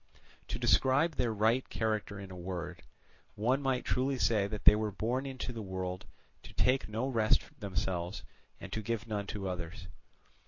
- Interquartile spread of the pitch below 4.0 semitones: No, average, 4.7 semitones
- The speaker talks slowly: No, average, 165 wpm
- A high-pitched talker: No, low, 110 Hz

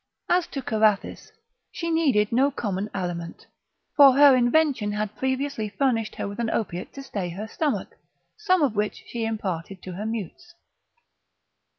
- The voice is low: No, high, 225 Hz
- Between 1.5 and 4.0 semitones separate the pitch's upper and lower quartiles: No, average, 5.3 semitones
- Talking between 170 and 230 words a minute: No, average, 155 wpm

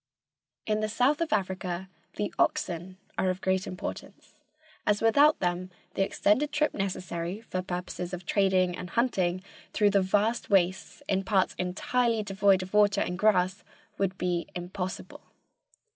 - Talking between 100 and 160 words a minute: Yes, average, 145 wpm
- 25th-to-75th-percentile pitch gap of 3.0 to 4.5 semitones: No, narrow, 2.5 semitones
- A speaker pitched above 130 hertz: Yes, high, 190 Hz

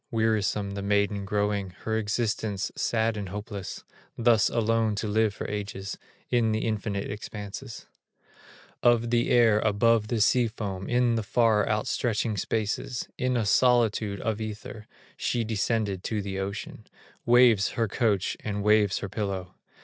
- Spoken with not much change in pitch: Yes, narrow, 2.1 semitones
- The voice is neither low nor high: No, low, 110 Hz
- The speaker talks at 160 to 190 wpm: No, average, 145 wpm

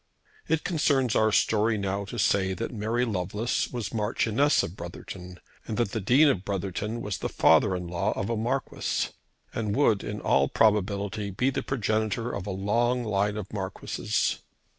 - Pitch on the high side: No, low, 105 Hz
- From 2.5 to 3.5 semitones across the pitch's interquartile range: Yes, average, 3.1 semitones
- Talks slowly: No, average, 170 wpm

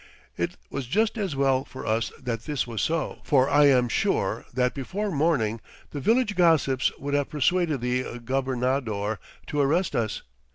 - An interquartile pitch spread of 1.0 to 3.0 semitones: No, average, 4.0 semitones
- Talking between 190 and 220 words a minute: No, average, 165 wpm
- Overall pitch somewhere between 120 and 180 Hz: Yes, low, 135 Hz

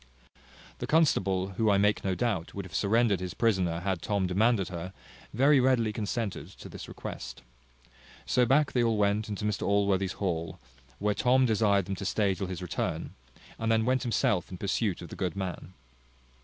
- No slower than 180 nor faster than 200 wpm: Yes, average, 185 wpm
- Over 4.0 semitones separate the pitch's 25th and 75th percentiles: No, average, 3.3 semitones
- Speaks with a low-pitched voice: Yes, low, 100 Hz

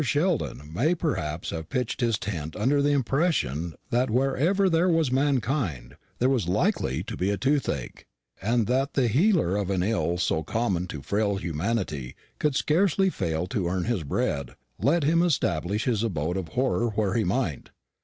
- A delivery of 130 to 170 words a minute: Yes, average, 165 wpm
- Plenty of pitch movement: Yes, wide, 8.3 semitones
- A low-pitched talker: Yes, low, 110 Hz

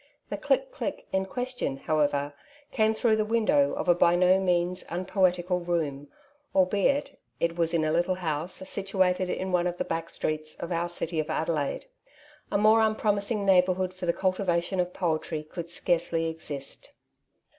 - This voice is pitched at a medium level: Yes, medium, 180 Hz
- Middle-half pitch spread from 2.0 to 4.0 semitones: Yes, average, 2.7 semitones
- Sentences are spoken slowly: No, average, 165 wpm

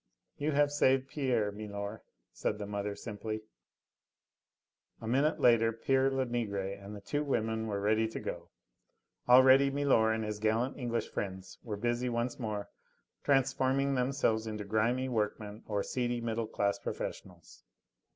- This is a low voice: Yes, low, 115 Hz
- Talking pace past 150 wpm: No, average, 140 wpm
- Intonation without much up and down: No, average, 3.8 semitones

